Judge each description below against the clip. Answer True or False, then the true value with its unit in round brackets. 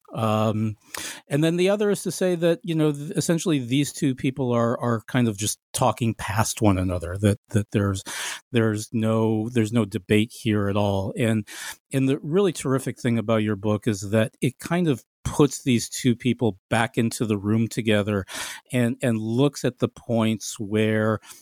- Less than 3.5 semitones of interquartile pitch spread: False (4.1 semitones)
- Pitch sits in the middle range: False (115 Hz)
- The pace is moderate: True (180 wpm)